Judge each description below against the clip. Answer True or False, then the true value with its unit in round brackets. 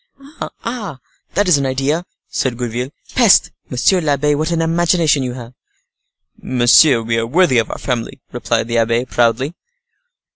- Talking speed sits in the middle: True (150 wpm)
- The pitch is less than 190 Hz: True (135 Hz)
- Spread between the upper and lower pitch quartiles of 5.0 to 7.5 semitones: True (5.4 semitones)